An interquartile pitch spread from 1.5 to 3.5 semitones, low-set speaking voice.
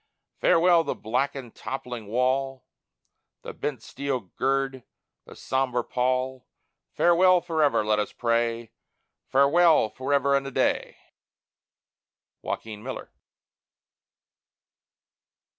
Yes: average, 2.7 semitones; low, 130 Hz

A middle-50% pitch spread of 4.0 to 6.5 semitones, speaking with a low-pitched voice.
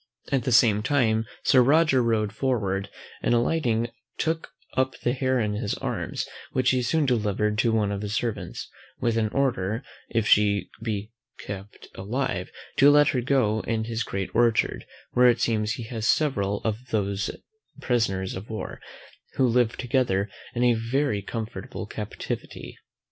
No: average, 3.3 semitones; low, 115 Hz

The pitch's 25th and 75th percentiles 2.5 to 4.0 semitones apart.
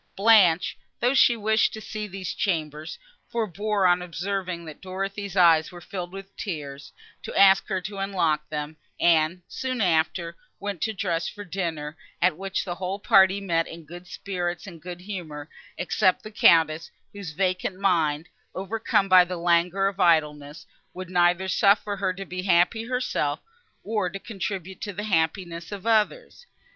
Yes: average, 2.9 semitones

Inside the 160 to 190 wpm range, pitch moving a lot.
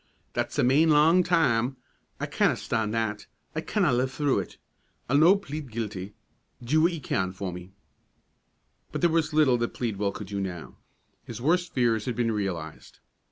Yes: average, 175 wpm; wide, 6.8 semitones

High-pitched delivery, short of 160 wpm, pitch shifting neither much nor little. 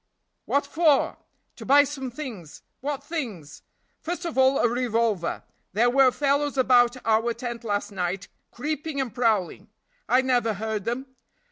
Yes: high, 245 Hz; average, 145 wpm; average, 4.0 semitones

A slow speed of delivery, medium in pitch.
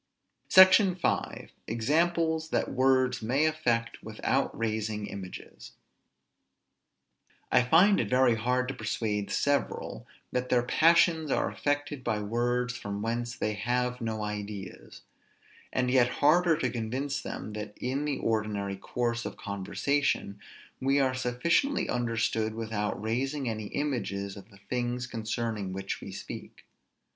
No: slow, 130 wpm; low, 120 Hz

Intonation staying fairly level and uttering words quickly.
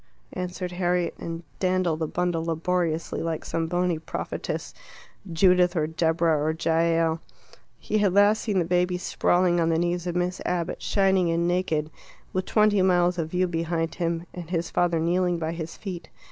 No: narrow, 1.6 semitones; average, 170 wpm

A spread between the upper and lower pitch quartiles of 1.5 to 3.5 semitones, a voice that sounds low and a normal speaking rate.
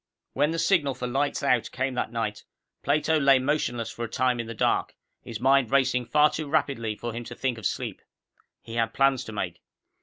No: average, 3.2 semitones; low, 130 Hz; fast, 210 wpm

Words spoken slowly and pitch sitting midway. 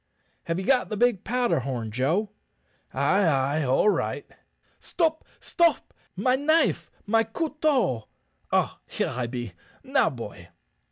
No: slow, 130 wpm; high, 200 Hz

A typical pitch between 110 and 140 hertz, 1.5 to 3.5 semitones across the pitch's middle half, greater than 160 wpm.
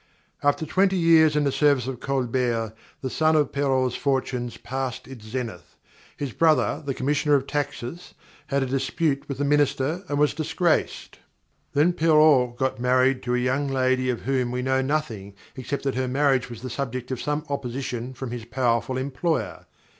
Yes: low, 135 Hz; narrow, 2.6 semitones; average, 175 wpm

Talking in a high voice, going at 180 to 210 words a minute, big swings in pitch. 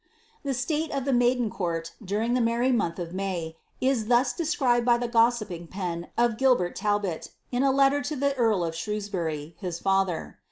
Yes: high, 230 Hz; average, 185 wpm; wide, 5.8 semitones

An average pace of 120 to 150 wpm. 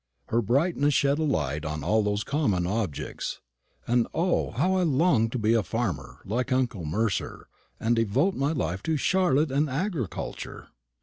No: average, 165 wpm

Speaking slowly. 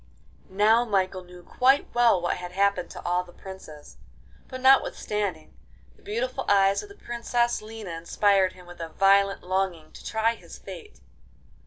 No: average, 160 wpm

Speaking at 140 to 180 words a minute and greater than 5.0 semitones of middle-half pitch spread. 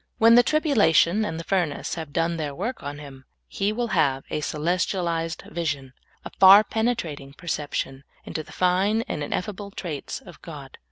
Yes: average, 165 wpm; wide, 5.6 semitones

